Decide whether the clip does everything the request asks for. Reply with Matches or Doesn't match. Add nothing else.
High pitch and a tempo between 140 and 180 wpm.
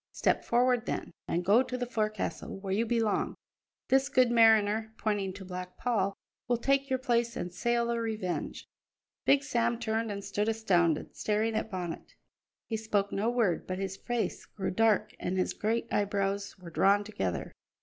Matches